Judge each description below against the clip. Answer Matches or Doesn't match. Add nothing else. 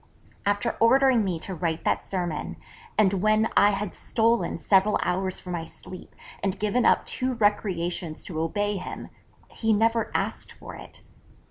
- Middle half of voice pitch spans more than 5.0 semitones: Doesn't match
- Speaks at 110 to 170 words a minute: Matches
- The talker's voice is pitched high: Matches